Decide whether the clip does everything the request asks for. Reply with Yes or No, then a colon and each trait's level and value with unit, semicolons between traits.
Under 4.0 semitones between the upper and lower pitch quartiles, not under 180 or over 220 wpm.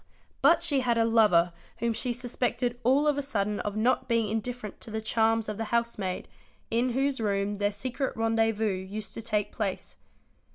Yes: average, 2.7 semitones; average, 190 wpm